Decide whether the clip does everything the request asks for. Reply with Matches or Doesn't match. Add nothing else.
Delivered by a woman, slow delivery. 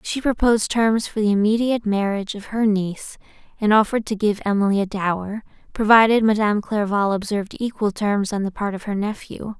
Doesn't match